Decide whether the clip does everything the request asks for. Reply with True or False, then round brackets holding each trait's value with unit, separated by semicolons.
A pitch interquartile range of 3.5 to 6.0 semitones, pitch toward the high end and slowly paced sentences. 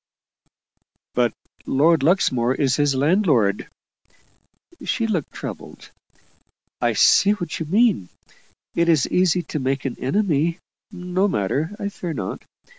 False (5.6 semitones; 160 Hz; 120 wpm)